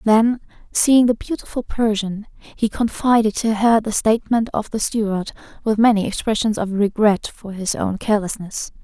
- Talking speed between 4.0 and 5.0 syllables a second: Yes, 4.8 syllables/s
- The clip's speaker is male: No, female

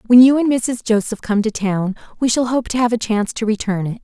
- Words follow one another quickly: Yes, fast, 270 wpm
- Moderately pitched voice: No, high, 225 Hz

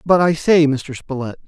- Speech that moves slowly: No, fast, 205 wpm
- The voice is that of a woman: No, male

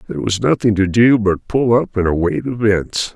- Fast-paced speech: Yes, fast, 210 wpm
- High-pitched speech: No, low, 105 Hz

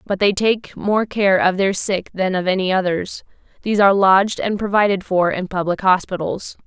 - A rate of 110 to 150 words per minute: No, average, 190 wpm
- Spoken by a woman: Yes, female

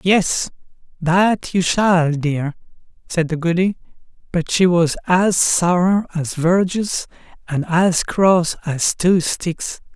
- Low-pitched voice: No, medium, 175 Hz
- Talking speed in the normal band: No, slow, 125 wpm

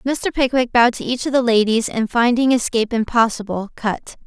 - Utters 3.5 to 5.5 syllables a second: Yes, 5.4 syllables/s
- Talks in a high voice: Yes, high, 240 Hz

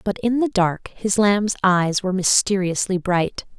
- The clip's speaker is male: No, female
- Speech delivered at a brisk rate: No, average, 165 wpm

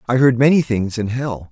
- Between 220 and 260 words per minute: Yes, fast, 240 wpm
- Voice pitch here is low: Yes, low, 120 Hz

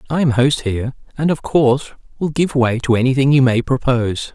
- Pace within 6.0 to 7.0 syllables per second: No, 5.5 syllables/s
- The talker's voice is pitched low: Yes, low, 130 Hz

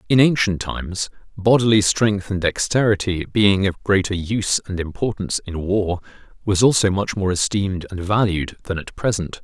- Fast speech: No, average, 160 wpm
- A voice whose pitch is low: Yes, low, 100 Hz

